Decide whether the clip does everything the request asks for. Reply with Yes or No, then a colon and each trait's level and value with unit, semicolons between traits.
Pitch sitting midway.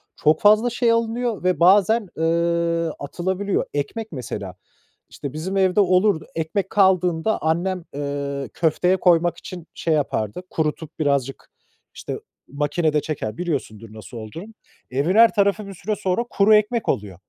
Yes: medium, 170 Hz